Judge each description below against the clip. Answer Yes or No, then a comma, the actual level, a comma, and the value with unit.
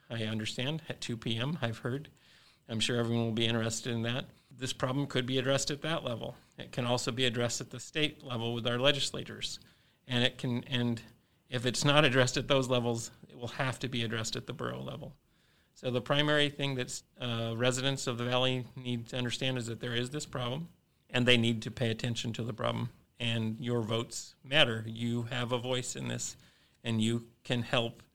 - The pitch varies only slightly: Yes, narrow, 2.3 semitones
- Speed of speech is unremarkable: No, fast, 210 wpm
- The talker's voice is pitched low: Yes, low, 125 Hz